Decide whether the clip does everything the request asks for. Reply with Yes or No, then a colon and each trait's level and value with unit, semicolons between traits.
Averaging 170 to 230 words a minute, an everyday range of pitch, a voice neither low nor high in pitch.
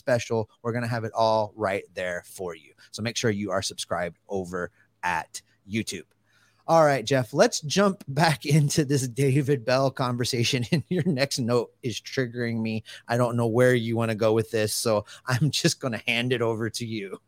No: average, 200 wpm; average, 3.9 semitones; low, 120 Hz